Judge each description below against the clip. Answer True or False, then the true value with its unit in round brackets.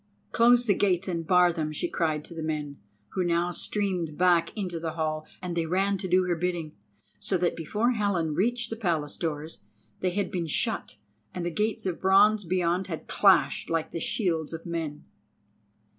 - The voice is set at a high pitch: False (175 Hz)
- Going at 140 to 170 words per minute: False (190 wpm)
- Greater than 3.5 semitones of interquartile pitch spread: False (3.0 semitones)